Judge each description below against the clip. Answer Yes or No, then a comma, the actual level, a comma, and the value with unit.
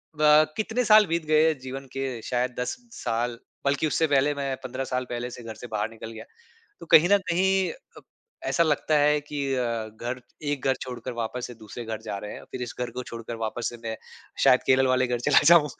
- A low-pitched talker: Yes, low, 130 Hz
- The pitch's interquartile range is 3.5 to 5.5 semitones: Yes, average, 4.0 semitones